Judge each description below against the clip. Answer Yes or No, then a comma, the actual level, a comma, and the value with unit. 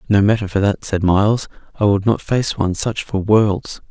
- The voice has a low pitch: Yes, low, 105 Hz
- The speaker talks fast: Yes, fast, 215 wpm